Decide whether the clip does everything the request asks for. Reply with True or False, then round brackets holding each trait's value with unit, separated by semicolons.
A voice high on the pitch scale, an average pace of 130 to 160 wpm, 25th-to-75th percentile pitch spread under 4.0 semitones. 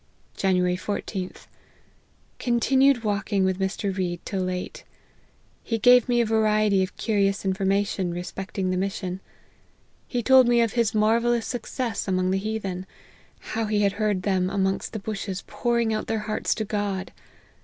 True (205 Hz; 150 wpm; 2.8 semitones)